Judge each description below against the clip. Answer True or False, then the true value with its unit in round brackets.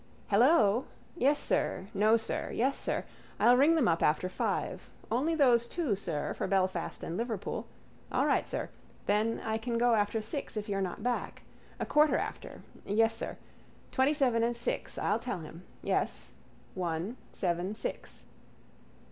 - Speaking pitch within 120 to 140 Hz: False (225 Hz)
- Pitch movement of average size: True (4.1 semitones)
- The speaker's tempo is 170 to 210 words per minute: False (155 wpm)